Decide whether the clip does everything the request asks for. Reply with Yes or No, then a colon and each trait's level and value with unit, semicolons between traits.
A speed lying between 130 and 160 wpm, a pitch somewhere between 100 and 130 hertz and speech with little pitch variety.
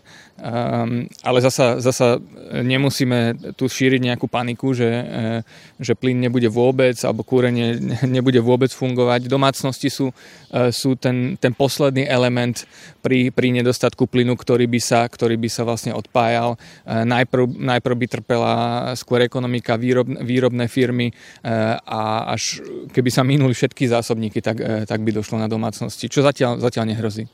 Yes: average, 140 wpm; low, 125 Hz; narrow, 1.6 semitones